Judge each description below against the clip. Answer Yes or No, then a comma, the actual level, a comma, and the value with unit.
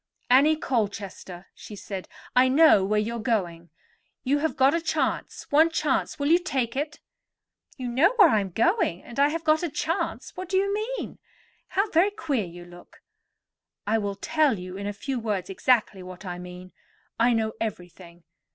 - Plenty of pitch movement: Yes, wide, 8.3 semitones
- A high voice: Yes, high, 235 Hz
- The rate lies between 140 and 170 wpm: No, average, 180 wpm